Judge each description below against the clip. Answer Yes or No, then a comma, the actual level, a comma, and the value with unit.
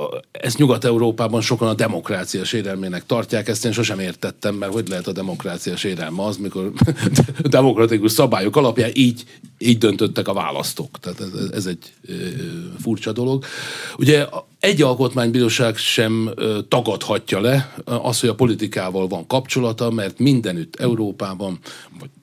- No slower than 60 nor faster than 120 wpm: No, average, 135 wpm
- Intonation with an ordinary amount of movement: Yes, average, 3.3 semitones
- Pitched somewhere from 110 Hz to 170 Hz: Yes, low, 115 Hz